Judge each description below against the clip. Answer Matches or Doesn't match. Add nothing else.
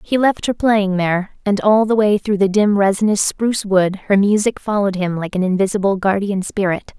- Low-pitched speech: Doesn't match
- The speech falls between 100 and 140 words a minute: Doesn't match